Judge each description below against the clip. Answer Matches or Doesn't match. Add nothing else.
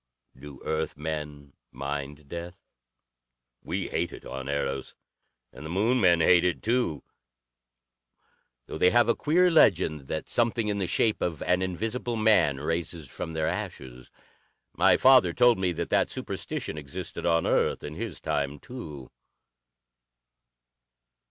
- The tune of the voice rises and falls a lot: Matches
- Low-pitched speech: Matches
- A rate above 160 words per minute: Doesn't match